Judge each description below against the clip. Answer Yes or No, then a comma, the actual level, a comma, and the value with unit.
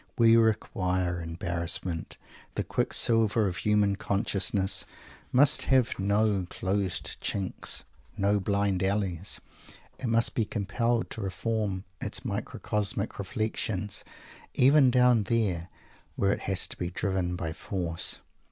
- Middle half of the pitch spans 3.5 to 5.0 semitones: No, average, 3.1 semitones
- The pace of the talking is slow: Yes, slow, 115 wpm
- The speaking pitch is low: Yes, low, 100 Hz